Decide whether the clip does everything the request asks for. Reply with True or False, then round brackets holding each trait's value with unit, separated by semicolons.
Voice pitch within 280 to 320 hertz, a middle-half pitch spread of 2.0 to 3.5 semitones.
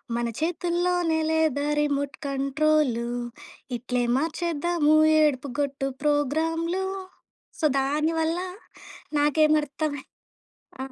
True (300 Hz; 2.6 semitones)